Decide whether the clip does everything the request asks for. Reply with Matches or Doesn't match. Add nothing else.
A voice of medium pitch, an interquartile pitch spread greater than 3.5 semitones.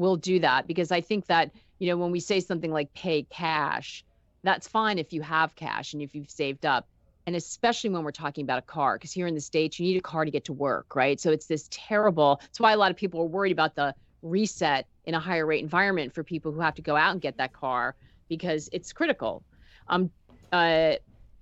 Doesn't match